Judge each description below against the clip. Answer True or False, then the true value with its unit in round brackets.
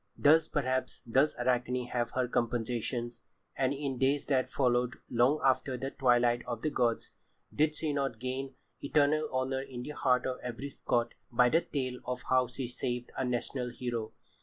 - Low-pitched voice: True (125 Hz)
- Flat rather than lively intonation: True (1.9 semitones)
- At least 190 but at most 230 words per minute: False (170 wpm)